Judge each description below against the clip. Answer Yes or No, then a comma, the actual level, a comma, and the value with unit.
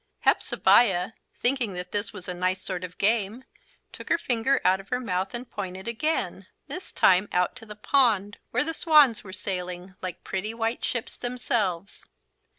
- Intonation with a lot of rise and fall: No, average, 4.6 semitones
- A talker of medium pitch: No, high, 205 Hz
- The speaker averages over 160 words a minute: Yes, average, 175 wpm